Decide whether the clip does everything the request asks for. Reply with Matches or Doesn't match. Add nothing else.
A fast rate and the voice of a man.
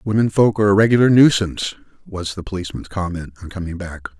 Doesn't match